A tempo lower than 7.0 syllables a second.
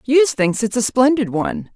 Yes: 5.5 syllables/s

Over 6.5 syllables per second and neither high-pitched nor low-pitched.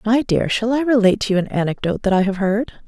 No: 6.9 syllables/s; high, 215 Hz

